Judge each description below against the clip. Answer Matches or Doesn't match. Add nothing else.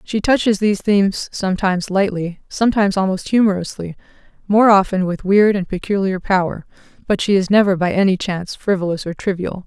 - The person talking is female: Matches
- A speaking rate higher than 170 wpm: Doesn't match